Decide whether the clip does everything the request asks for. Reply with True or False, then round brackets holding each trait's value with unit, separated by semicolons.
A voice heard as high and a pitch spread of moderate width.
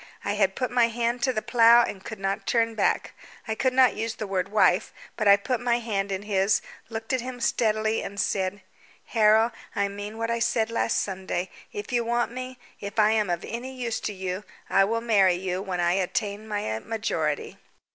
True (215 Hz; 3.1 semitones)